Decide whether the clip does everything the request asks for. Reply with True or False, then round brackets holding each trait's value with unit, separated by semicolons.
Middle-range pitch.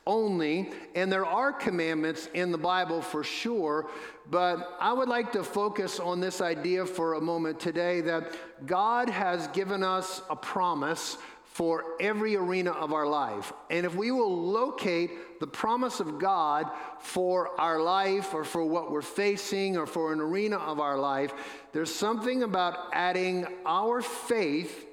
True (175 Hz)